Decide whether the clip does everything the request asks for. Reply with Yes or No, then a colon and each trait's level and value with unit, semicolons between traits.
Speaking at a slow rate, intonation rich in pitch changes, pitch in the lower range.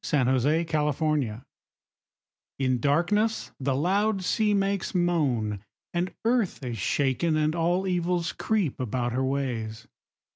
No: slow, 115 wpm; wide, 5.7 semitones; medium, 155 Hz